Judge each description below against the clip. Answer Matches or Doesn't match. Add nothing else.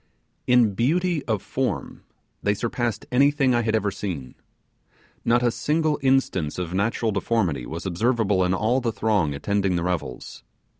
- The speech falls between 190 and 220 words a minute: Doesn't match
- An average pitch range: Matches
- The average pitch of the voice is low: Matches